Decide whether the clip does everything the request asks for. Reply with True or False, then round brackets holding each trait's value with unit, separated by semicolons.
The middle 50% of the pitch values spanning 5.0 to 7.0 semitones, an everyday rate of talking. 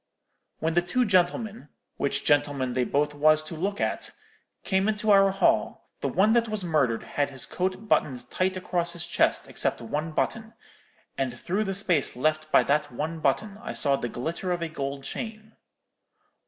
True (5.5 semitones; 170 wpm)